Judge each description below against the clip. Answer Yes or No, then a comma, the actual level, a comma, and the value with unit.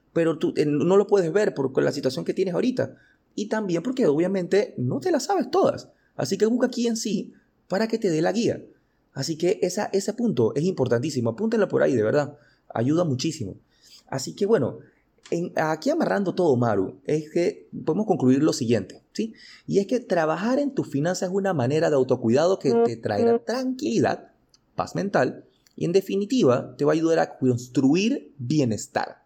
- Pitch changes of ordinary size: No, wide, 7.0 semitones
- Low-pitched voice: No, medium, 180 Hz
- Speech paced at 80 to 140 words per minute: No, fast, 190 wpm